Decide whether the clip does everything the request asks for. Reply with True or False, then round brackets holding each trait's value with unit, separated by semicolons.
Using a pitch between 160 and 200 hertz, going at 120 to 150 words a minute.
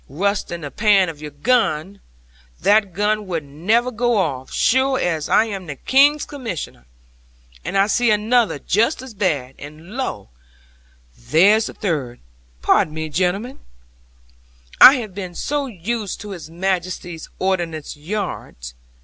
True (190 Hz; 140 wpm)